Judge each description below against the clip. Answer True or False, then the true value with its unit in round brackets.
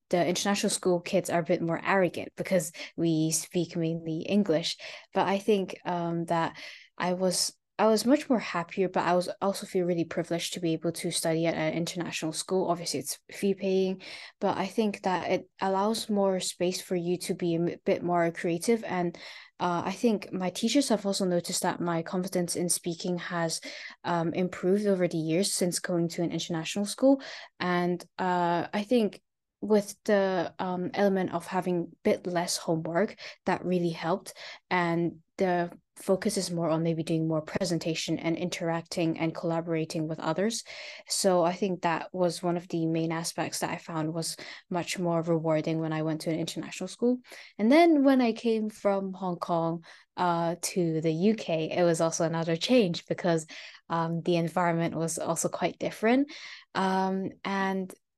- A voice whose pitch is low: False (175 Hz)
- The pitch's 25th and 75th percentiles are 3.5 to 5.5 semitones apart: False (2.5 semitones)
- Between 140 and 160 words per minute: False (175 wpm)